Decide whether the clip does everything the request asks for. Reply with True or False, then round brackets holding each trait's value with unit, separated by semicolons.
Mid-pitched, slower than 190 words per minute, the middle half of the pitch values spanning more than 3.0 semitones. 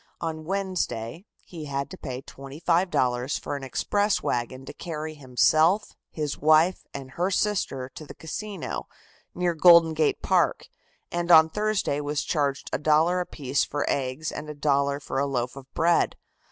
True (155 Hz; 160 wpm; 4.0 semitones)